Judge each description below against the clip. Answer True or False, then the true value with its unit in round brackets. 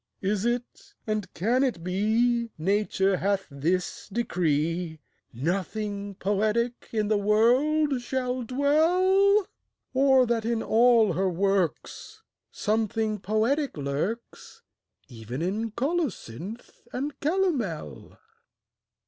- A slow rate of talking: True (100 wpm)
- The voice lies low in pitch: False (220 Hz)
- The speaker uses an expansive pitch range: False (4.9 semitones)